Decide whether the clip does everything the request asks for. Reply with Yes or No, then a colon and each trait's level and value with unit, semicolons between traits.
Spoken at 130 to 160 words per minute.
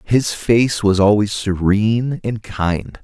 Yes: average, 140 wpm